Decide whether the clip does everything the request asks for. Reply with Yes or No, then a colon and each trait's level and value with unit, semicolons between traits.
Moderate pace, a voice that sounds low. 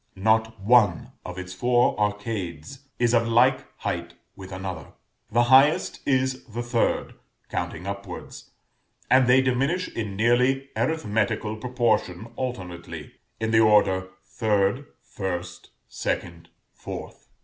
No: slow, 115 wpm; low, 110 Hz